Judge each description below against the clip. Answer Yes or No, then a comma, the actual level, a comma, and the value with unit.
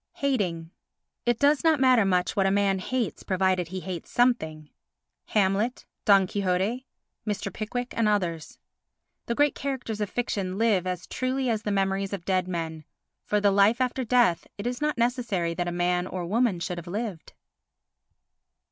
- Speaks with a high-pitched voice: Yes, high, 200 Hz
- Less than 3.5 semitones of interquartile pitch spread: No, average, 4.9 semitones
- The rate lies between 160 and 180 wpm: Yes, average, 165 wpm